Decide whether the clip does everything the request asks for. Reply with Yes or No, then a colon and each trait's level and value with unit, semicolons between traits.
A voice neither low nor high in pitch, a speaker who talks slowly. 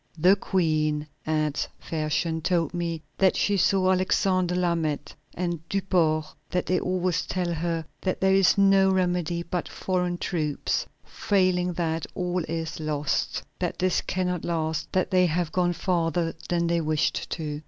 No: medium, 175 Hz; average, 150 wpm